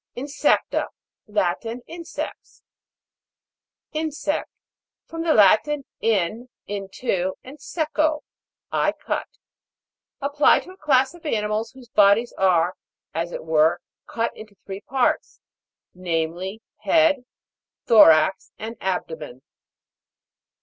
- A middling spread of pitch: No, wide, 7.3 semitones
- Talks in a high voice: Yes, high, 225 Hz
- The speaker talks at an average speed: No, slow, 100 wpm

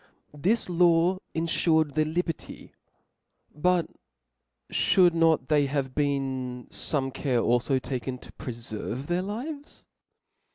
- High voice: No, medium, 150 Hz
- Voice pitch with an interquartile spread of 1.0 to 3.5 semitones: No, average, 4.7 semitones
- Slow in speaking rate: Yes, slow, 110 wpm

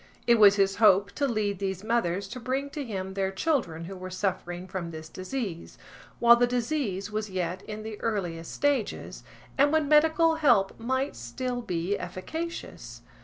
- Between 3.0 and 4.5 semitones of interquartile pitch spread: No, wide, 5.5 semitones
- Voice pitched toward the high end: Yes, high, 210 Hz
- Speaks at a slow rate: No, average, 170 wpm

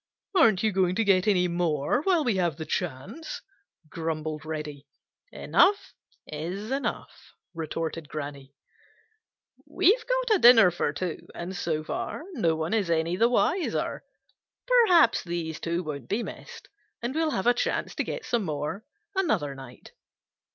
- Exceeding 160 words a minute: No, average, 150 wpm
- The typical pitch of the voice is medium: Yes, medium, 180 Hz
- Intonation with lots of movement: Yes, wide, 7.4 semitones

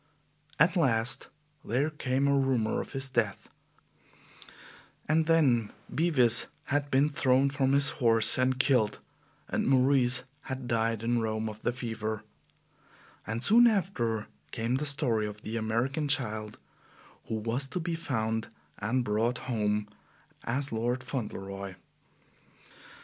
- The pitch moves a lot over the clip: No, average, 3.9 semitones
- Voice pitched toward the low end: Yes, low, 125 Hz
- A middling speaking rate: No, slow, 130 wpm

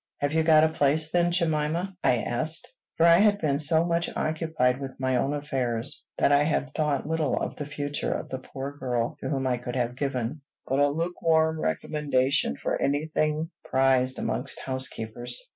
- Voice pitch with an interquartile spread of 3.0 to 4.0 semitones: Yes, average, 3.5 semitones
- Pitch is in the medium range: Yes, medium, 145 Hz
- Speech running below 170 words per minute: No, average, 185 wpm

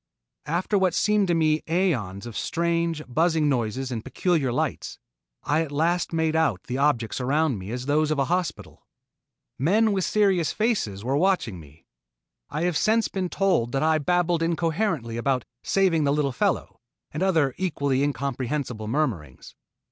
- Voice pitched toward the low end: No, medium, 155 Hz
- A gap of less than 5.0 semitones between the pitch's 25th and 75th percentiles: No, wide, 5.4 semitones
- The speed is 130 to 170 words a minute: Yes, average, 160 wpm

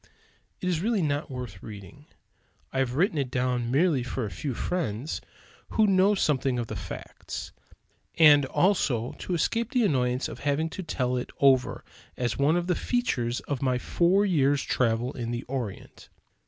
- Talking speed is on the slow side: No, average, 170 wpm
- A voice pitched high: No, low, 135 Hz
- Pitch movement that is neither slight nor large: No, wide, 5.8 semitones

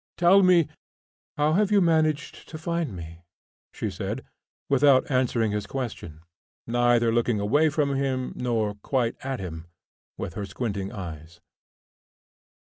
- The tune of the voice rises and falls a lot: Yes, wide, 6.4 semitones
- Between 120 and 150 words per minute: Yes, average, 140 wpm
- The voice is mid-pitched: No, low, 125 Hz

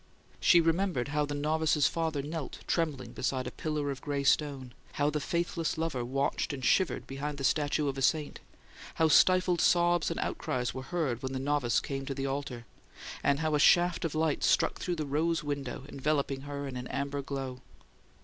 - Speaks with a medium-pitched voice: Yes, medium, 145 Hz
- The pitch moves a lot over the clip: No, average, 2.8 semitones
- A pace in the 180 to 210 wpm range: Yes, average, 190 wpm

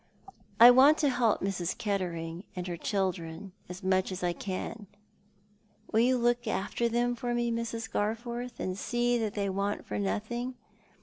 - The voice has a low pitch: No, high, 210 Hz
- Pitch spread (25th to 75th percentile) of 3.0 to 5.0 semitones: Yes, average, 4.5 semitones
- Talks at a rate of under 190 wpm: Yes, average, 165 wpm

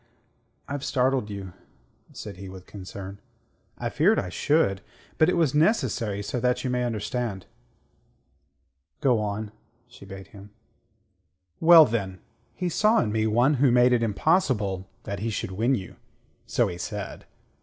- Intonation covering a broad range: No, average, 5.0 semitones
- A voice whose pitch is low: Yes, low, 110 Hz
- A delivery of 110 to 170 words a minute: Yes, average, 150 wpm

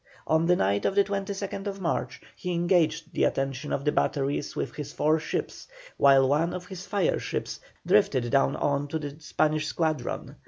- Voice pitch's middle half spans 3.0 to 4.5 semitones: Yes, average, 4.0 semitones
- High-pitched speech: No, medium, 155 Hz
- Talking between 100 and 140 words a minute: No, average, 180 wpm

